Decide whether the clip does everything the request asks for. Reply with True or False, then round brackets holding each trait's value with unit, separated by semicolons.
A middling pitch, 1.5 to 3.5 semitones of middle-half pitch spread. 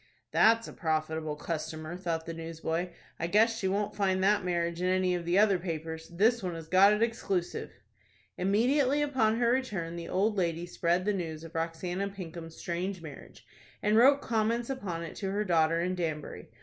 False (180 Hz; 4.0 semitones)